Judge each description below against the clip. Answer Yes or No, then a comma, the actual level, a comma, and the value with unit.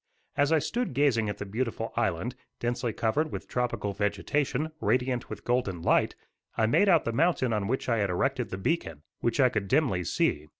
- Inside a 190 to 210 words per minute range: Yes, average, 195 wpm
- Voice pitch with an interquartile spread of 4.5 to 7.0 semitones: Yes, average, 5.1 semitones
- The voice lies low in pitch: Yes, low, 120 Hz